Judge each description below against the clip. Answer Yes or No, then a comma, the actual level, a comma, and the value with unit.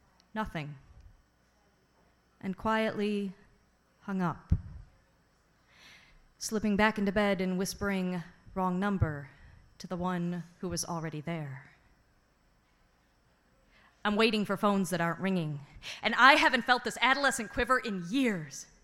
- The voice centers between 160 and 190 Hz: Yes, medium, 185 Hz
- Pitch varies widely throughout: Yes, wide, 6.2 semitones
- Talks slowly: Yes, slow, 115 wpm